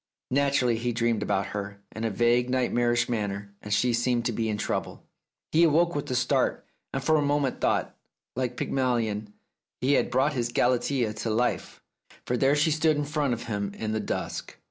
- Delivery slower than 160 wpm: No, average, 195 wpm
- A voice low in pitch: Yes, low, 120 Hz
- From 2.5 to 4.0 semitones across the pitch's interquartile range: Yes, average, 3.7 semitones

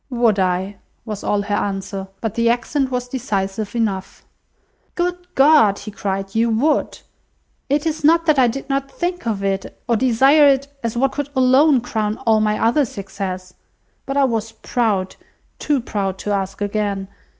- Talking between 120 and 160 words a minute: No, average, 170 wpm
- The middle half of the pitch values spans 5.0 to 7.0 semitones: Yes, average, 5.3 semitones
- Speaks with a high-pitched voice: Yes, high, 225 Hz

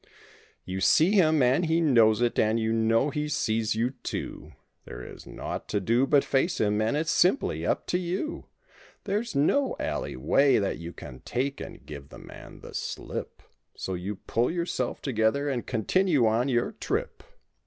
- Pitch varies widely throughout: Yes, wide, 6.1 semitones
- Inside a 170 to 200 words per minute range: Yes, average, 180 wpm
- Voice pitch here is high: No, low, 125 Hz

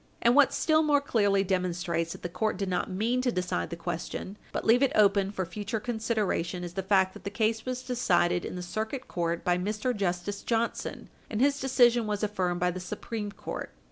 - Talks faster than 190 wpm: Yes, fast, 205 wpm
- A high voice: Yes, high, 205 Hz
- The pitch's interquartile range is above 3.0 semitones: Yes, average, 4.5 semitones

